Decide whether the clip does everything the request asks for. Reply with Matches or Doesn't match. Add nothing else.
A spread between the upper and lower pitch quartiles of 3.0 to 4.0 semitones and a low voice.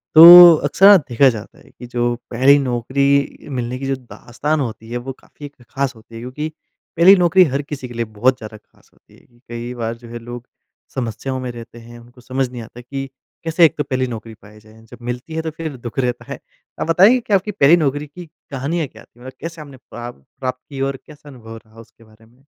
Matches